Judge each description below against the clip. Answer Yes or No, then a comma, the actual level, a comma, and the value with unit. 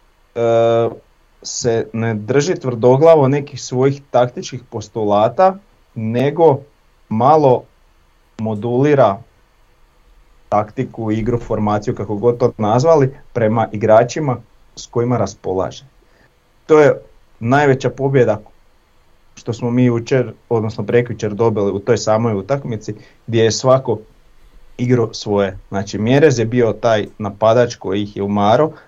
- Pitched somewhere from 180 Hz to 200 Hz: No, low, 115 Hz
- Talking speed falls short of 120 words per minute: Yes, slow, 110 wpm